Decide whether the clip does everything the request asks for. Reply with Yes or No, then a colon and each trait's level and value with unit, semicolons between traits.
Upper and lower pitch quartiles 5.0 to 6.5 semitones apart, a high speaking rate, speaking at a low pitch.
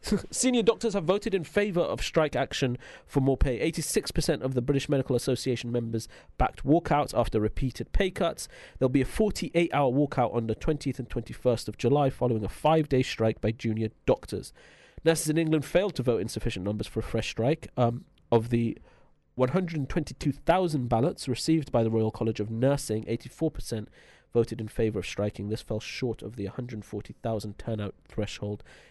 No: wide, 5.6 semitones; average, 175 wpm; low, 125 Hz